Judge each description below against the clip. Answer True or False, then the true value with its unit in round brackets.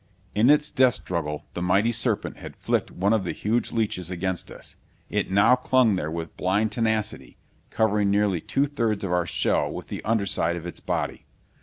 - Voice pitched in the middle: False (105 Hz)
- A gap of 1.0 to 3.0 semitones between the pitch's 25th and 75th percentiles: False (4.0 semitones)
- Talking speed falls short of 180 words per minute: False (185 wpm)